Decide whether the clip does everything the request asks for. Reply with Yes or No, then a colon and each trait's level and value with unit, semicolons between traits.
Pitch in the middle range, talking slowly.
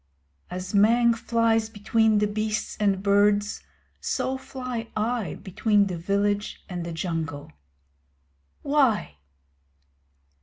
No: high, 210 Hz; slow, 105 wpm